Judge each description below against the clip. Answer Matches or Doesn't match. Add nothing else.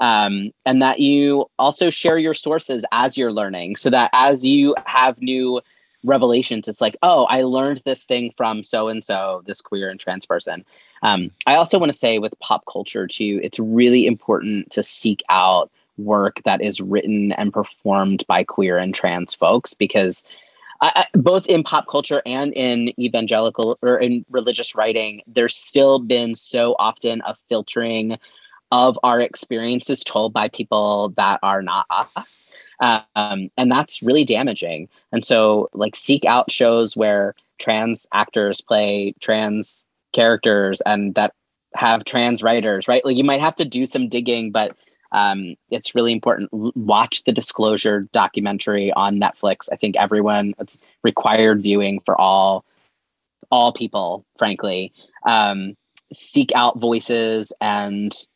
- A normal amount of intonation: Matches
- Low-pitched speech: Matches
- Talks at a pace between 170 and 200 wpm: Doesn't match